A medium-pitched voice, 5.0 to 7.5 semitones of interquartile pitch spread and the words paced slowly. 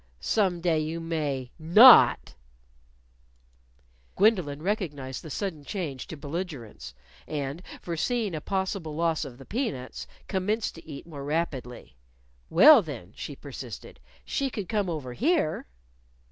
Yes: medium, 160 Hz; wide, 5.4 semitones; slow, 125 wpm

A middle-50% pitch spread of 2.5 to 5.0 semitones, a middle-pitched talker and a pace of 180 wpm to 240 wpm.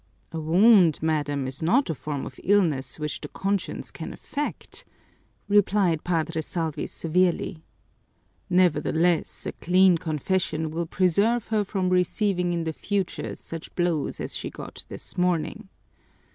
No: average, 3.2 semitones; medium, 175 Hz; slow, 135 wpm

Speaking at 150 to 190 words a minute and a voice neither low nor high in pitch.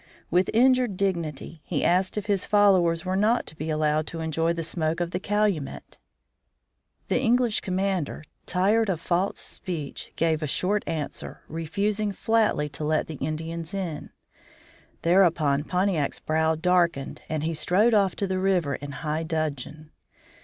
Yes: average, 155 wpm; medium, 170 Hz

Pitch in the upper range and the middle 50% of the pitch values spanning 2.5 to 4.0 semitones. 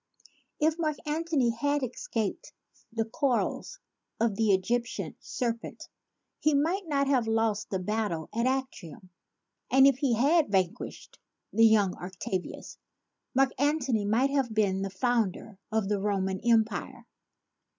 No: high, 230 Hz; average, 5.2 semitones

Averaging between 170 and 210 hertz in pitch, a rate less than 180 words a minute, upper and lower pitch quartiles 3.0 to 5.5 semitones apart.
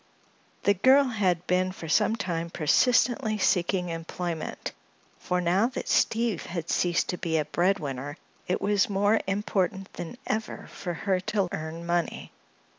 Yes: medium, 185 Hz; average, 145 wpm; average, 3.4 semitones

